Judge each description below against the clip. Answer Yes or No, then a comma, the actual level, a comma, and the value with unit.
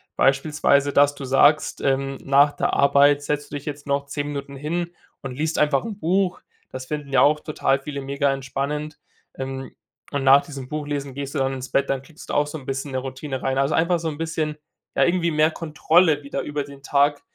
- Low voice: No, medium, 145 Hz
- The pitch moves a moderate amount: No, narrow, 1.7 semitones